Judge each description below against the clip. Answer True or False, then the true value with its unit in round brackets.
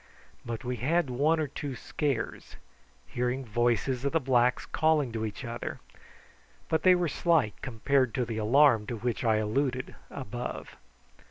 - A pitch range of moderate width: True (3.4 semitones)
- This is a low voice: True (125 Hz)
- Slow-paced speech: False (155 wpm)